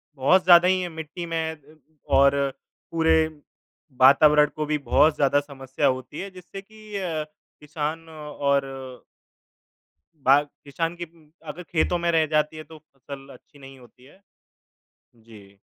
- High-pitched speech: No, medium, 155 Hz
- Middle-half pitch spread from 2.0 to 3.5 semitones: Yes, average, 3.2 semitones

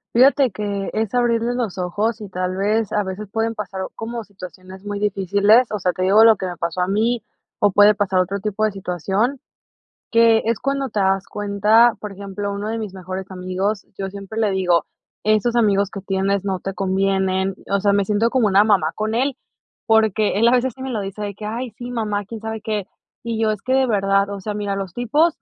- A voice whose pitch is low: No, high, 205 Hz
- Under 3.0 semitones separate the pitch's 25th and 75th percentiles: Yes, narrow, 2.5 semitones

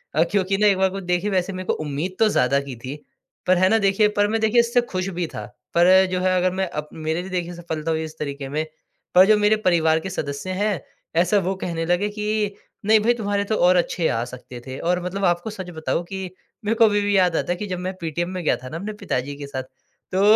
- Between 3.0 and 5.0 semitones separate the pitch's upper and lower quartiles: Yes, average, 4.0 semitones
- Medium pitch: Yes, medium, 180 Hz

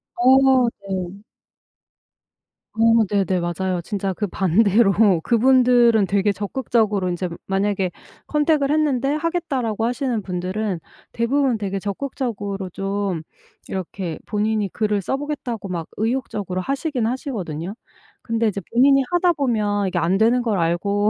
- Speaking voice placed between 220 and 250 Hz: No, high, 210 Hz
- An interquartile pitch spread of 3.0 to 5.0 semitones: Yes, average, 4.5 semitones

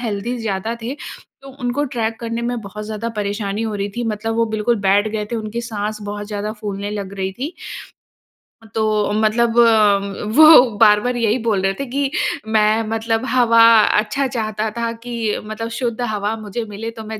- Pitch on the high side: Yes, high, 220 Hz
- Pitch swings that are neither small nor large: No, narrow, 2.0 semitones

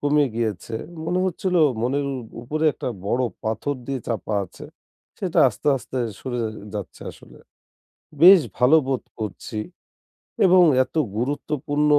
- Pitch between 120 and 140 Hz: Yes, low, 135 Hz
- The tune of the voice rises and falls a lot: No, average, 4.4 semitones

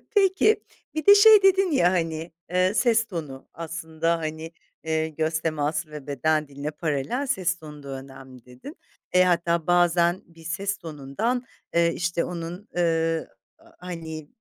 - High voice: No, medium, 165 Hz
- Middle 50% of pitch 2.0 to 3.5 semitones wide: Yes, average, 2.9 semitones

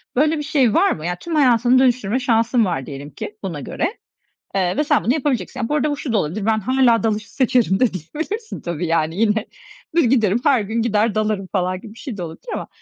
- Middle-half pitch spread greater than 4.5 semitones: Yes, wide, 5.4 semitones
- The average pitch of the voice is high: Yes, high, 225 Hz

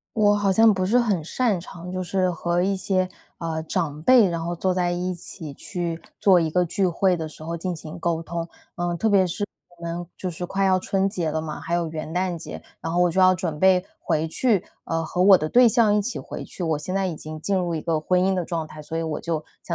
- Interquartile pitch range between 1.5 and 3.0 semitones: Yes, narrow, 2.5 semitones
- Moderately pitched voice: Yes, medium, 175 Hz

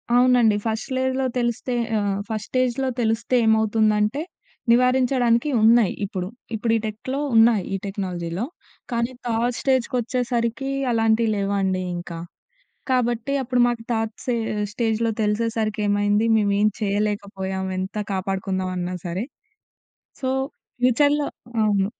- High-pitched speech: Yes, high, 225 Hz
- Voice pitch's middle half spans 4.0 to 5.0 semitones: No, average, 3.1 semitones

